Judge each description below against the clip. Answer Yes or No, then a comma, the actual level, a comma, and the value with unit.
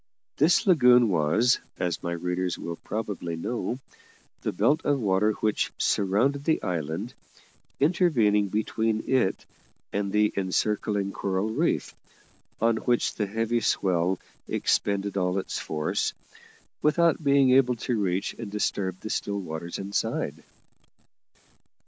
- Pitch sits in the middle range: No, low, 105 Hz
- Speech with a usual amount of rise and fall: Yes, average, 4.5 semitones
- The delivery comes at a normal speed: No, slow, 125 wpm